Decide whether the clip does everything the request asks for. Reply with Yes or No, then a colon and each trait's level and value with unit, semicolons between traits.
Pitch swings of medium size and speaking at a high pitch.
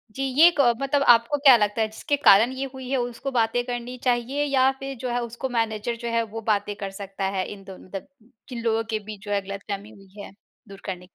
Yes: average, 3.8 semitones; high, 230 Hz